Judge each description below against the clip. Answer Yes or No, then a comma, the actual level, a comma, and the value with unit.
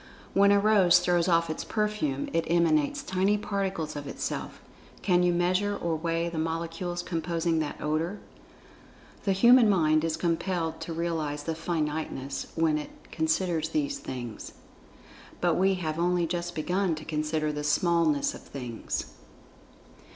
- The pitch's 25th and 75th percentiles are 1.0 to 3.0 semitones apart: Yes, average, 2.7 semitones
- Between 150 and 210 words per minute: No, average, 140 wpm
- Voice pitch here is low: No, medium, 165 Hz